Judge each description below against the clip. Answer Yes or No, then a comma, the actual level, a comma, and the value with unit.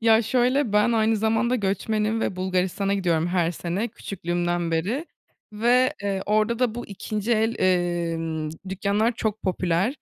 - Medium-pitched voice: No, high, 205 Hz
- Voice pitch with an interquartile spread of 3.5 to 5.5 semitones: Yes, average, 4.1 semitones